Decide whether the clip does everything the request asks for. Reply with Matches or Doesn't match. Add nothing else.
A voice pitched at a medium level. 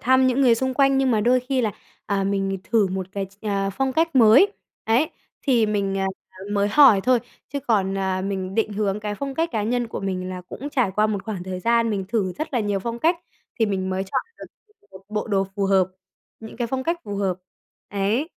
Doesn't match